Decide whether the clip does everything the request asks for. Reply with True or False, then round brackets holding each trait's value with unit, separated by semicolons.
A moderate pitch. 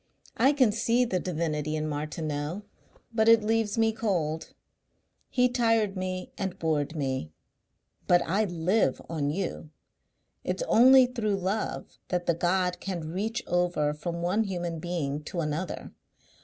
True (180 Hz)